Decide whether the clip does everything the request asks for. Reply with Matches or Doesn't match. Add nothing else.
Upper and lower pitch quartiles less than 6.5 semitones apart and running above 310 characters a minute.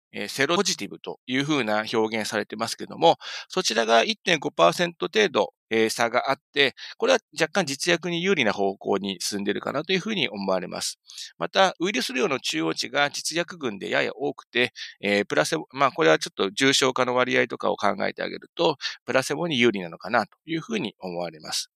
Doesn't match